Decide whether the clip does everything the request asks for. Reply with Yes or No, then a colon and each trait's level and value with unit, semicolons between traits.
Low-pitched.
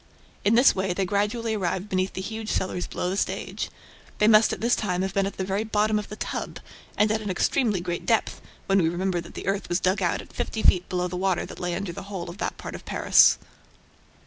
No: high, 195 Hz